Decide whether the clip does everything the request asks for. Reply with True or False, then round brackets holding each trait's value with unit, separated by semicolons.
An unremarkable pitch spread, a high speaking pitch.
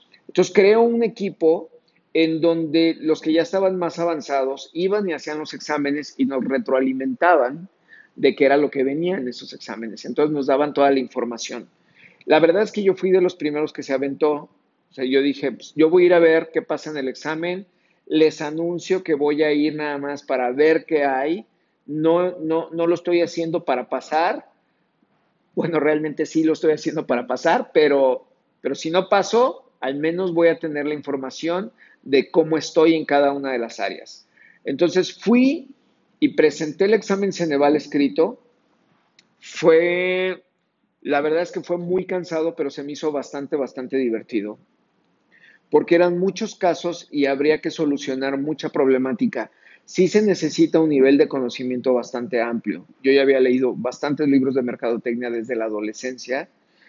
False (4.2 semitones; 155 Hz)